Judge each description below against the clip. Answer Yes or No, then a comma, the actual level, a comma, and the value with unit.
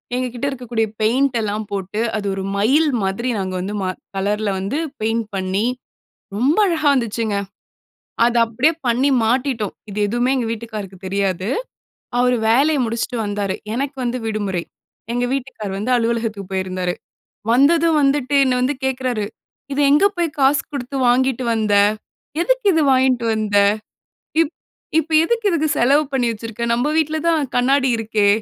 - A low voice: No, high, 240 Hz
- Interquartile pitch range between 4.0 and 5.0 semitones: Yes, average, 4.5 semitones